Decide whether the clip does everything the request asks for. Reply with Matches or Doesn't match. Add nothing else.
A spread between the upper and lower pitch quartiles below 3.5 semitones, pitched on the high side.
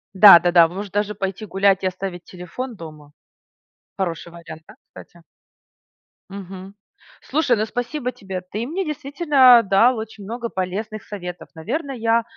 Doesn't match